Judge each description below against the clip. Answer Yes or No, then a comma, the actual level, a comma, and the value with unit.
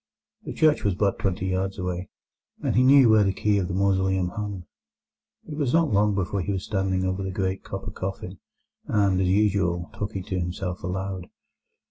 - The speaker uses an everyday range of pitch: No, narrow, 1.8 semitones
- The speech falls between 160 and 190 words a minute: Yes, average, 185 wpm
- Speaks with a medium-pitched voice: No, very low, 95 Hz